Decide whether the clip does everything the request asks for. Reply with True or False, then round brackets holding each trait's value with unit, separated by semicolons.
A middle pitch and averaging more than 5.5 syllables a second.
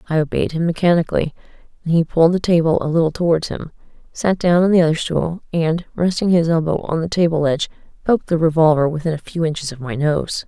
True (165 Hz; 6.3 syllables/s)